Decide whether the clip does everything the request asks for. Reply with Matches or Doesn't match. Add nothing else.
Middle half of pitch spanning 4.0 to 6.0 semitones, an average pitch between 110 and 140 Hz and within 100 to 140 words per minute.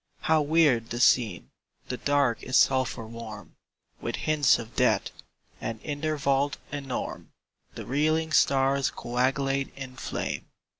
Doesn't match